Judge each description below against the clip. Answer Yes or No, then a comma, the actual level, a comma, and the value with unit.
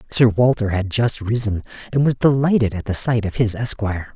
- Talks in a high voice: No, low, 110 Hz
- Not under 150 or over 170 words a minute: No, average, 200 wpm